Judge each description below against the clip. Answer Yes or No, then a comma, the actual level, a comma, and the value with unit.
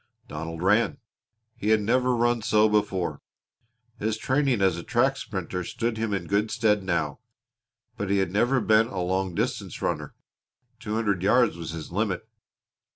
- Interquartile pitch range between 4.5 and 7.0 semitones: No, average, 3.4 semitones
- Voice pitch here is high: No, low, 105 Hz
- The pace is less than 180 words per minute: Yes, average, 160 wpm